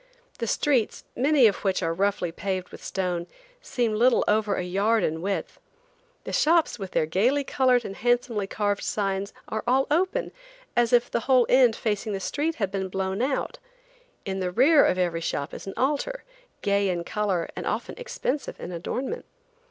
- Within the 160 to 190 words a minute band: Yes, average, 180 wpm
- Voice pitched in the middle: No, high, 210 Hz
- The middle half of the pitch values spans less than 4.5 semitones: No, average, 5.1 semitones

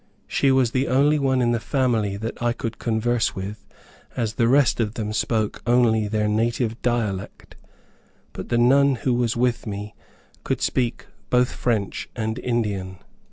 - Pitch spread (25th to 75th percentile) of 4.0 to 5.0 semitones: No, narrow, 2.5 semitones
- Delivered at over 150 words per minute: Yes, average, 160 wpm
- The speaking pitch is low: Yes, low, 115 Hz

